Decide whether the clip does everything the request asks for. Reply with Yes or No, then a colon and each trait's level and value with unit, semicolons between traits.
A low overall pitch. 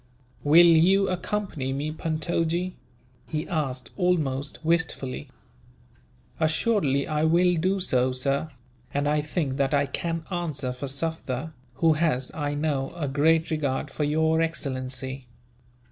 No: medium, 155 Hz